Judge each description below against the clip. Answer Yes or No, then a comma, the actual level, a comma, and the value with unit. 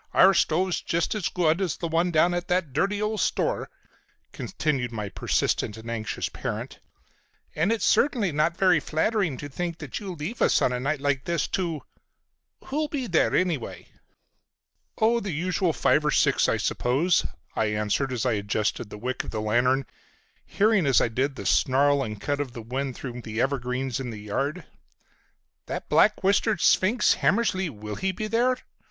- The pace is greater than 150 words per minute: Yes, average, 175 wpm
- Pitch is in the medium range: Yes, medium, 150 Hz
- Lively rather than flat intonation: Yes, wide, 7.0 semitones